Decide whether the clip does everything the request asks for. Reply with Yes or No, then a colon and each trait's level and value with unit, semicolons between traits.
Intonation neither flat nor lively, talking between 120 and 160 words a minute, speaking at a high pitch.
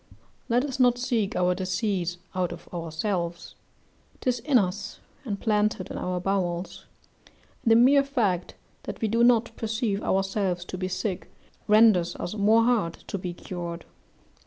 Yes: average, 4.1 semitones; average, 155 wpm; high, 200 Hz